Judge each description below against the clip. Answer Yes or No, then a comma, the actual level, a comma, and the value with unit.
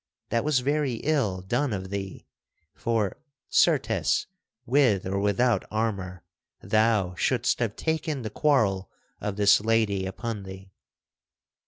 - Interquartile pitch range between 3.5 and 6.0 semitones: Yes, average, 4.2 semitones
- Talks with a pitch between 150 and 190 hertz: No, low, 110 Hz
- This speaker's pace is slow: Yes, slow, 125 wpm